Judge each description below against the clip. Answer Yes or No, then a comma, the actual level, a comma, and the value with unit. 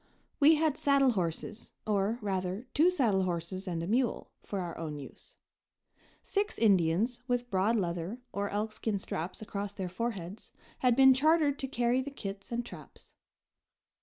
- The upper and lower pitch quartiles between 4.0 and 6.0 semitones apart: Yes, average, 5.2 semitones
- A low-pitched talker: No, high, 210 Hz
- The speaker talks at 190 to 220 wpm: No, average, 155 wpm